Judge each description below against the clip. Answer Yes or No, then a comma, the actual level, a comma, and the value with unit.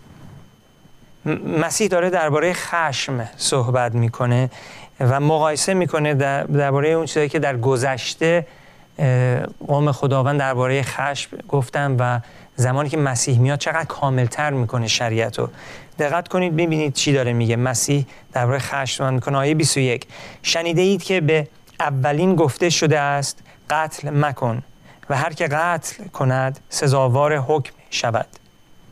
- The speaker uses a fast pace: No, average, 125 wpm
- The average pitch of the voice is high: No, medium, 140 Hz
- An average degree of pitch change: Yes, average, 3.3 semitones